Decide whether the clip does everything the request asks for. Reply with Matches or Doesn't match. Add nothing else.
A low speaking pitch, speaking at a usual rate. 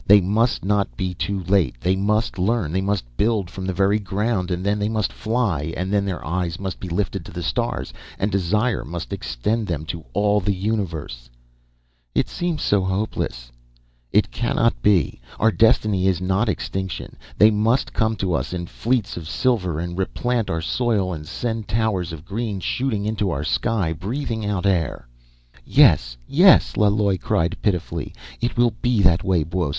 Matches